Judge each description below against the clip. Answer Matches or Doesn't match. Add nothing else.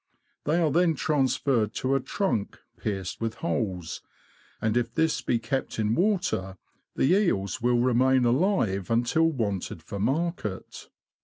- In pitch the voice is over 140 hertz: Doesn't match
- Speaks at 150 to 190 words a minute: Doesn't match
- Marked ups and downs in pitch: Matches